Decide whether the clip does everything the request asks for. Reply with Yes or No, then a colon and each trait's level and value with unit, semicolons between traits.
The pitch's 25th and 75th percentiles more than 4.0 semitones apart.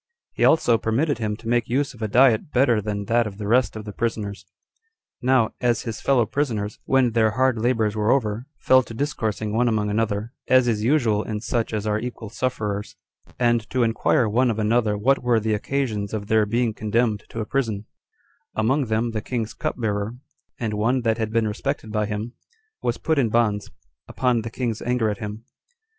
No: narrow, 2.4 semitones